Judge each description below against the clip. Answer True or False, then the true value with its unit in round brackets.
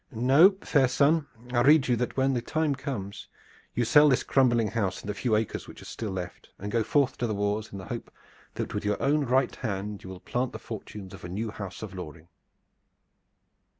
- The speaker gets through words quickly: True (220 wpm)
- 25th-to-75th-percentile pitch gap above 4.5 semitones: True (4.9 semitones)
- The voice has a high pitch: False (115 Hz)